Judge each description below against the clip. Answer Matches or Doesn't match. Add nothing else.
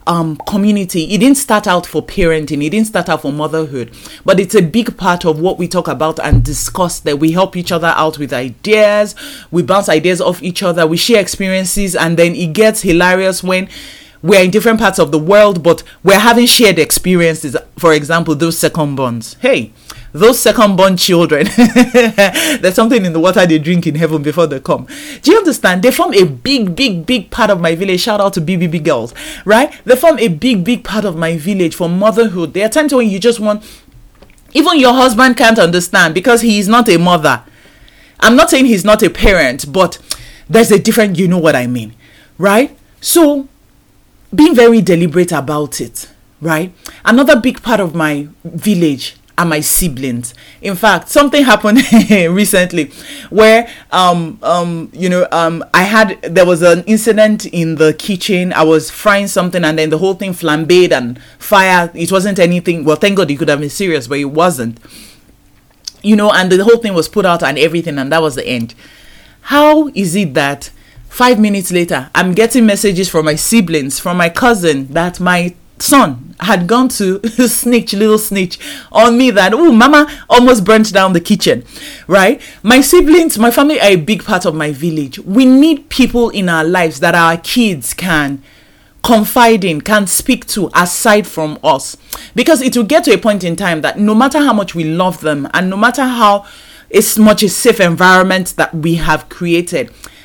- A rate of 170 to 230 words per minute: Matches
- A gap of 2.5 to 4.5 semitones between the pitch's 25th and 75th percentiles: Doesn't match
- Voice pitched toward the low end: Doesn't match